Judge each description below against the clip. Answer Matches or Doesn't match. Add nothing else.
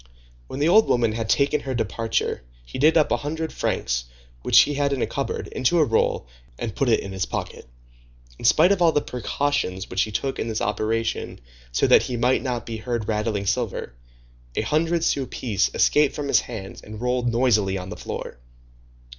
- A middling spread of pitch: Matches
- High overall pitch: Doesn't match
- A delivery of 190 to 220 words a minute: Matches